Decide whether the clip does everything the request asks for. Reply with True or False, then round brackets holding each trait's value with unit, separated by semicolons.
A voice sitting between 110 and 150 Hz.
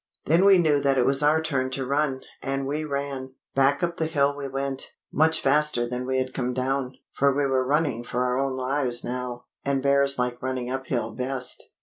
True (135 Hz)